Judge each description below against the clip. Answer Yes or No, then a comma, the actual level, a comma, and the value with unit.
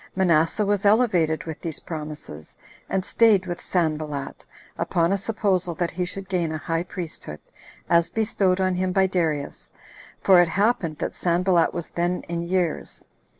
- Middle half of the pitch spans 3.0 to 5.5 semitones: No, narrow, 2.6 semitones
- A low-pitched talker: No, medium, 175 Hz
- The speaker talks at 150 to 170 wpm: Yes, average, 155 wpm